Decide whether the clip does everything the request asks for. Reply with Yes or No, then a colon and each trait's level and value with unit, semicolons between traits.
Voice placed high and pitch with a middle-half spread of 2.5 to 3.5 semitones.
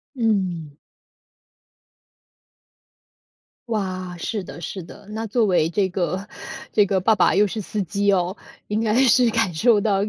Yes: high, 200 Hz; average, 2.9 semitones